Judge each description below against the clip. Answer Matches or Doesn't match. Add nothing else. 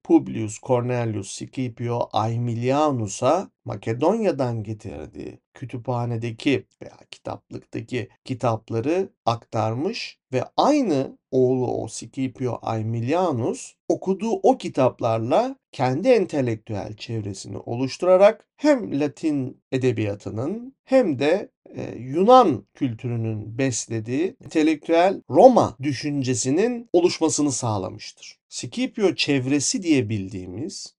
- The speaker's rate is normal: Doesn't match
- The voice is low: Matches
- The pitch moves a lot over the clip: Matches